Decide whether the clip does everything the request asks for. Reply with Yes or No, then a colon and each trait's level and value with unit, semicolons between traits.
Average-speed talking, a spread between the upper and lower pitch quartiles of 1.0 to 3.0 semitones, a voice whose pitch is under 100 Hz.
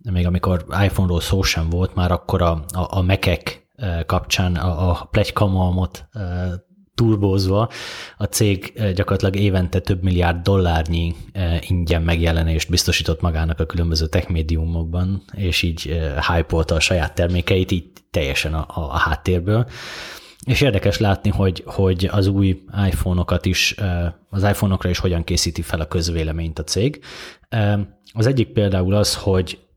Yes: average, 140 wpm; narrow, 2.6 semitones; very low, 90 Hz